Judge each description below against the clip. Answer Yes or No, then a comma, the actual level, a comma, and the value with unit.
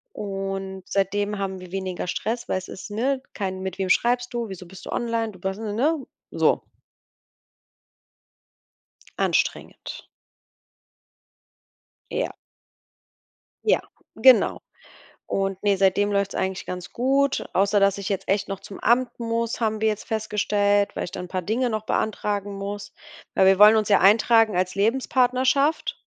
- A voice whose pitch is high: Yes, high, 205 Hz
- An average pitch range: Yes, average, 3.0 semitones